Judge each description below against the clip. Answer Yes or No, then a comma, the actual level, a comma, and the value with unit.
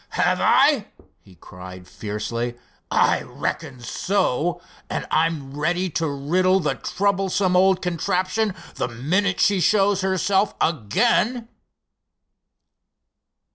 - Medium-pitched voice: Yes, medium, 180 Hz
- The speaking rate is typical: No, slow, 100 wpm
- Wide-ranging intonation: Yes, wide, 5.8 semitones